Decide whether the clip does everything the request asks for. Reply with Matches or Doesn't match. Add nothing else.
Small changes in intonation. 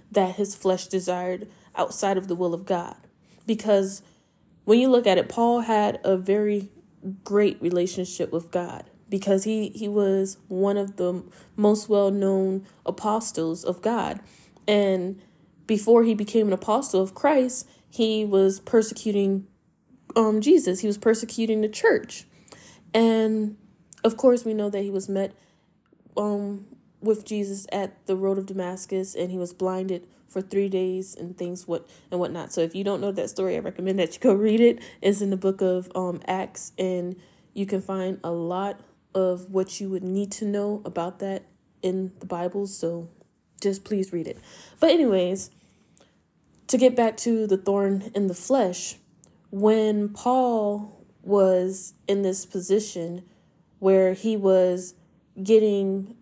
Matches